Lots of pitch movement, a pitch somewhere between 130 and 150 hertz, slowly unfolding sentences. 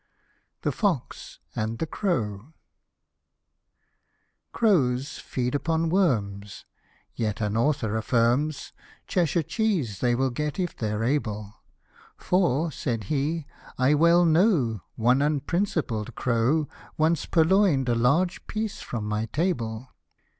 Yes: wide, 6.4 semitones; medium, 140 Hz; slow, 120 wpm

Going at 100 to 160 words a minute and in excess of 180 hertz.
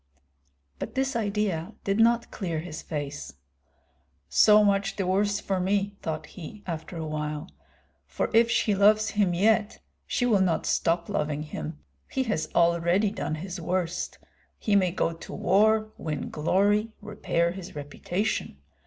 Yes: average, 150 wpm; high, 190 Hz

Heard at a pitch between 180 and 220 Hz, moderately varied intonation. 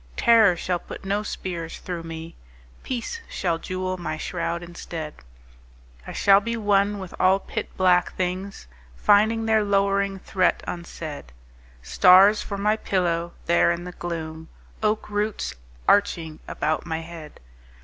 Yes: medium, 185 Hz; average, 3.2 semitones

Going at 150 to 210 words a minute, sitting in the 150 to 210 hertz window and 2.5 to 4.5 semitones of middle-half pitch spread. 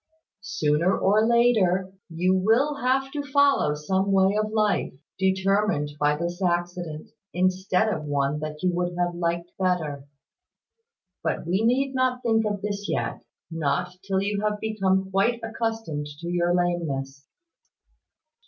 No: average, 140 wpm; high, 190 Hz; average, 3.8 semitones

